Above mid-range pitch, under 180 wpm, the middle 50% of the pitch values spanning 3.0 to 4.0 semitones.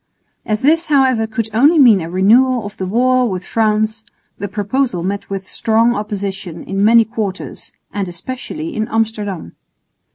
Yes: high, 220 Hz; average, 155 wpm; average, 3.7 semitones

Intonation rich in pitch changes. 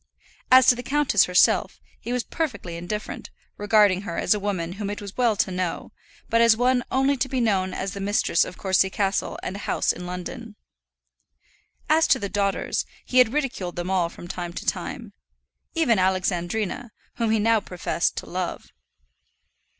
No: average, 4.4 semitones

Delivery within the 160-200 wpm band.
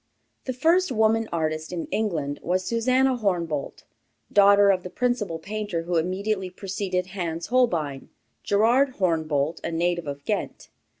No: slow, 135 wpm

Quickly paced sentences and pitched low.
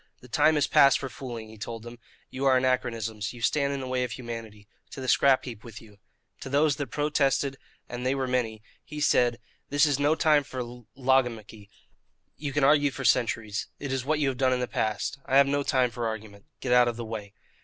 Yes: fast, 225 wpm; low, 130 Hz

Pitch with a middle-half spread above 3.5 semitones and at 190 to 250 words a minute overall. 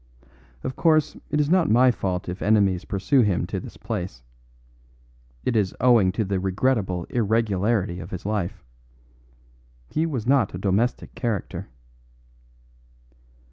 No: average, 4.9 semitones; slow, 135 wpm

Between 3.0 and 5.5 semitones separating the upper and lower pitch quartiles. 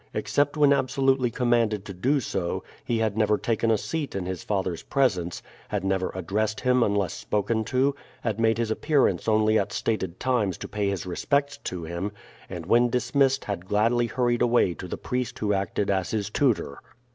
Yes: average, 4.4 semitones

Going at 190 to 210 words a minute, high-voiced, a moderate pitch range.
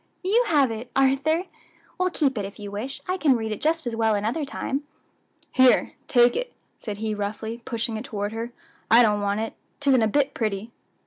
Yes: average, 200 wpm; high, 235 Hz; average, 4.4 semitones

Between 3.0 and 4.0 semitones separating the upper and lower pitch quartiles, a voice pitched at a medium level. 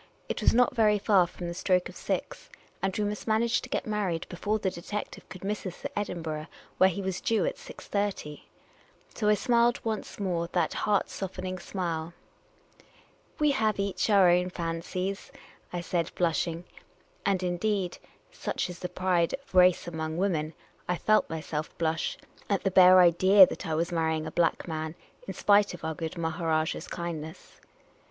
Yes: average, 3.4 semitones; medium, 180 Hz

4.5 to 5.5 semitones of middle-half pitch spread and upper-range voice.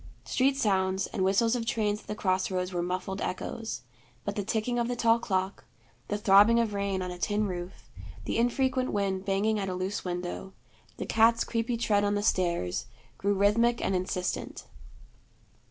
No: average, 3.3 semitones; high, 205 Hz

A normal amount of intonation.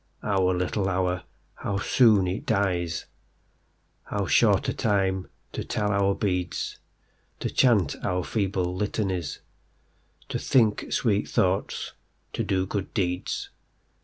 No: narrow, 2.1 semitones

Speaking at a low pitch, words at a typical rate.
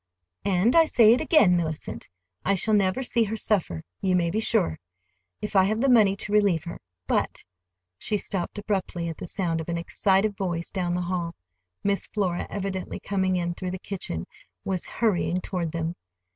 No: medium, 185 Hz; average, 180 wpm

